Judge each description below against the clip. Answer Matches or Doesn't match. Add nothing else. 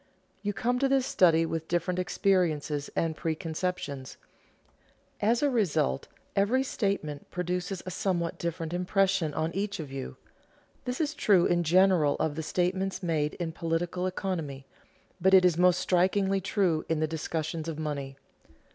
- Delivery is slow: Doesn't match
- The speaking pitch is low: Doesn't match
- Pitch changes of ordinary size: Matches